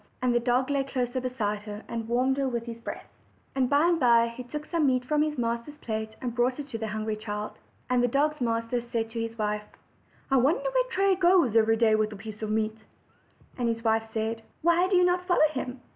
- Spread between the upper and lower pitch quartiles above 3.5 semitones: Yes, average, 4.1 semitones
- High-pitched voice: Yes, high, 240 Hz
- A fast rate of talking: Yes, fast, 235 wpm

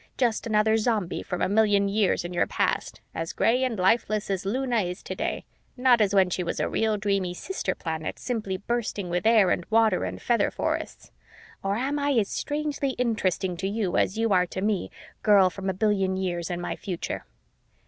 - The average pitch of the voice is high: Yes, high, 205 Hz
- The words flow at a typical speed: Yes, average, 195 wpm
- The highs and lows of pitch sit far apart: No, average, 3.5 semitones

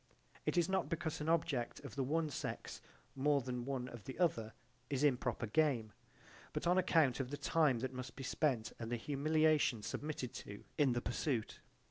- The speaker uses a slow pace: No, average, 185 wpm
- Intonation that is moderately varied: Yes, average, 4.1 semitones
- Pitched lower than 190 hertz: Yes, low, 135 Hz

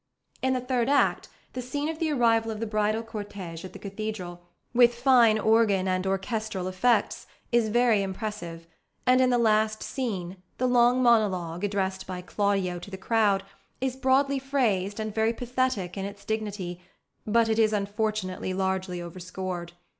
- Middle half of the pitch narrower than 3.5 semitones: No, average, 4.0 semitones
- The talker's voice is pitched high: Yes, high, 215 Hz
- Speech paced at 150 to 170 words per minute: Yes, average, 160 wpm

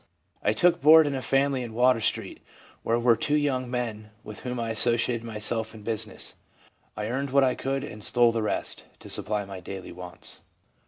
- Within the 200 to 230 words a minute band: Yes, fast, 205 wpm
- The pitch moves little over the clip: No, average, 3.4 semitones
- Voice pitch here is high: No, low, 115 Hz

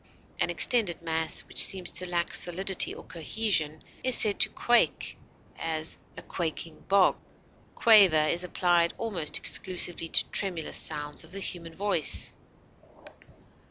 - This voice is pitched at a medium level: Yes, medium, 175 Hz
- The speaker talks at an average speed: No, slow, 130 wpm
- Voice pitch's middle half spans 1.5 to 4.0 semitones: Yes, average, 3.3 semitones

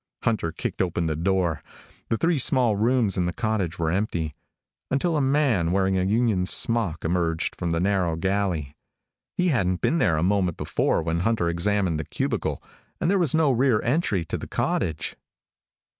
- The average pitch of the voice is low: Yes, very low, 95 Hz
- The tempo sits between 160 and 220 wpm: Yes, average, 175 wpm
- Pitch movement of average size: No, wide, 5.7 semitones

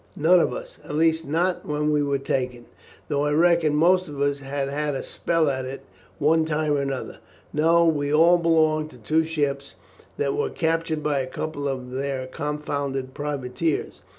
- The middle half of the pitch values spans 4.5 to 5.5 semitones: No, narrow, 2.6 semitones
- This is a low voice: No, medium, 150 Hz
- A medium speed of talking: Yes, average, 180 wpm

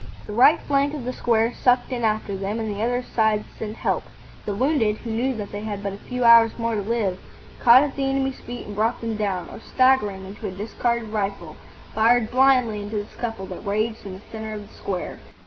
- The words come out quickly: Yes, fast, 225 wpm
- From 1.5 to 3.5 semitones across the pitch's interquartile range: Yes, average, 2.9 semitones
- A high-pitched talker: Yes, high, 220 Hz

